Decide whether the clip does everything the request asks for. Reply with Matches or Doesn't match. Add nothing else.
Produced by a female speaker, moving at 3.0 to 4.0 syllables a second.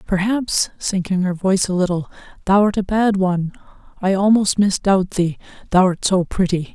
Matches